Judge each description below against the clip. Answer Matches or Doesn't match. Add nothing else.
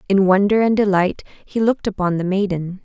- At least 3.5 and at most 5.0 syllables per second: Doesn't match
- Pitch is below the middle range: Doesn't match